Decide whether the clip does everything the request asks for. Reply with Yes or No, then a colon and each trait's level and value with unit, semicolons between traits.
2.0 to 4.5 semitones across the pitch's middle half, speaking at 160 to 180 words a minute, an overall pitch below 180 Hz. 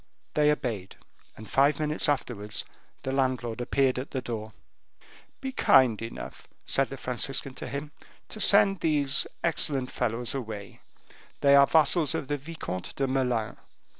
No: average, 3.6 semitones; average, 145 wpm; low, 135 Hz